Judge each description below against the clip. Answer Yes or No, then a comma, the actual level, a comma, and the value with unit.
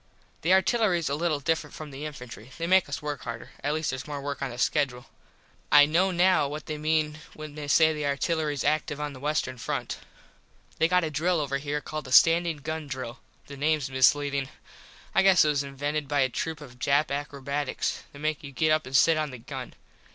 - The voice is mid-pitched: Yes, medium, 150 Hz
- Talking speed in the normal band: No, fast, 215 wpm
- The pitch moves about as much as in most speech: No, narrow, 2.1 semitones